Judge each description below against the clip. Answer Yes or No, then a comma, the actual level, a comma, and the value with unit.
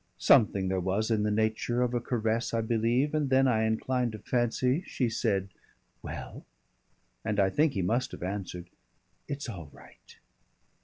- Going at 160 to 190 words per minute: Yes, average, 165 wpm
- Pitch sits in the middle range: No, low, 115 Hz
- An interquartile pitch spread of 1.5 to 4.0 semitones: Yes, average, 3.4 semitones